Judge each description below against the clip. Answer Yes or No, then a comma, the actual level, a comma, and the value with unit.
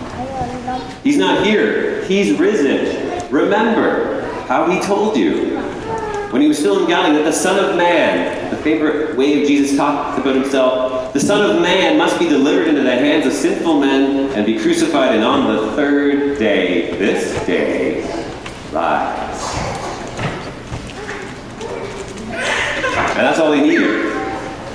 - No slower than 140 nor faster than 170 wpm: Yes, average, 145 wpm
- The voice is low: No, medium, 155 Hz